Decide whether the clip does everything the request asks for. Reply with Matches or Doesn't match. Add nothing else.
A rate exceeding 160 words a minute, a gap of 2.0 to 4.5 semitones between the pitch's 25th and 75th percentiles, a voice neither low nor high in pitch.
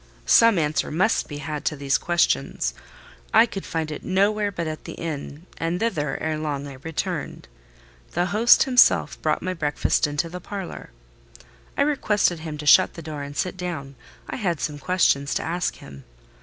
Matches